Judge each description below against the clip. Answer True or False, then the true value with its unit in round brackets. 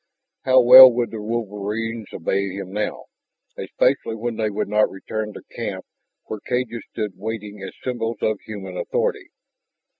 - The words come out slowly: False (150 wpm)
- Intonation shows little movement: True (2.3 semitones)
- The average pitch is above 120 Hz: False (110 Hz)